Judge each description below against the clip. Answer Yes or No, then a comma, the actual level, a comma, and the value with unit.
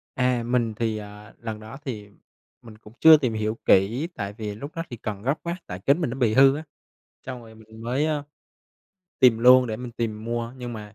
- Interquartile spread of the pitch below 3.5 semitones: Yes, average, 3.0 semitones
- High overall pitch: No, low, 115 Hz